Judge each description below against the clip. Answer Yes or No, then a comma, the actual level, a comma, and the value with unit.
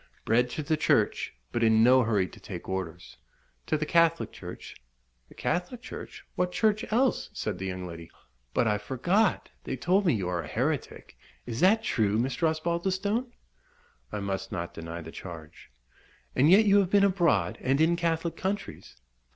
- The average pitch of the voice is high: No, medium, 150 Hz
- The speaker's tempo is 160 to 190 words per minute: Yes, average, 175 wpm